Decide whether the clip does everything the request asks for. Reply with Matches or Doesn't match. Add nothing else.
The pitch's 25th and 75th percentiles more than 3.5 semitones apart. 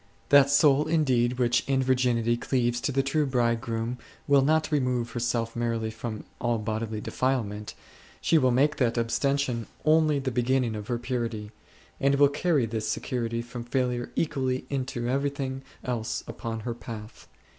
Doesn't match